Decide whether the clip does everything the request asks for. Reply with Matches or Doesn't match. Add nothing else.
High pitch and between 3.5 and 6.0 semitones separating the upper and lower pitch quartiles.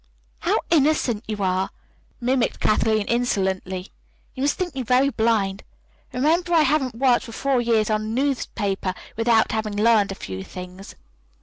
Matches